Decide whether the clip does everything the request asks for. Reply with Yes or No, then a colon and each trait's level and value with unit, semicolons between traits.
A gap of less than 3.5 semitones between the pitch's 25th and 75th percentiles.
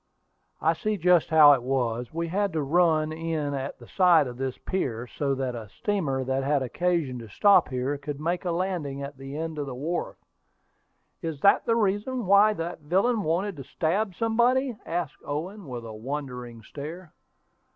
No: average, 5.2 semitones